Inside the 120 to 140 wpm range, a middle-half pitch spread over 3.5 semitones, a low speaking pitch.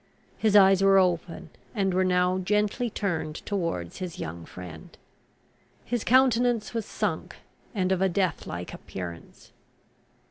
No: slow, 135 wpm; average, 4.0 semitones; medium, 185 Hz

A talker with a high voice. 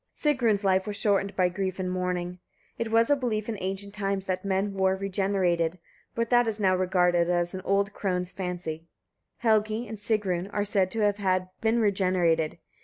Yes: high, 195 Hz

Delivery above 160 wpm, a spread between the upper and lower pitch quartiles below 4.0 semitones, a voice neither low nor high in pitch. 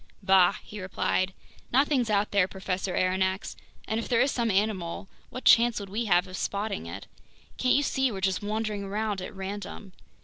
No: average, 180 wpm; average, 2.7 semitones; high, 200 Hz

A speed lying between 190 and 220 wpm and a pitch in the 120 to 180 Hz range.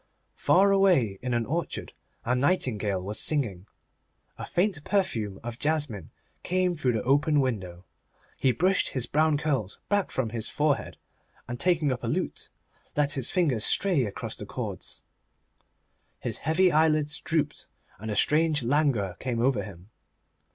No: average, 150 wpm; medium, 140 Hz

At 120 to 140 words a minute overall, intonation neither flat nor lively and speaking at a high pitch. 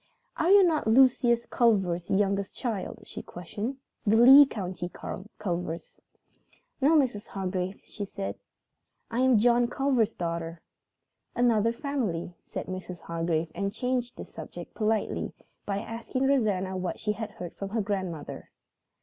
Yes: slow, 135 wpm; average, 4.7 semitones; high, 210 Hz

